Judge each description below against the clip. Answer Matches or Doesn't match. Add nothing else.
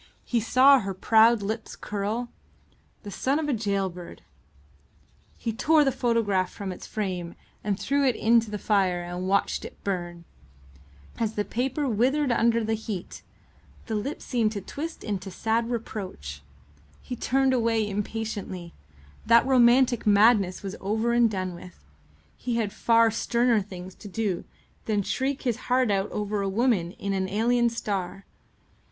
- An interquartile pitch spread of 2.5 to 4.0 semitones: Matches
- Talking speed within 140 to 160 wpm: Matches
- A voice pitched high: Matches